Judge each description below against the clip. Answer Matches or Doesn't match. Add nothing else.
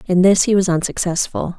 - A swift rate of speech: Doesn't match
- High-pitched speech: Doesn't match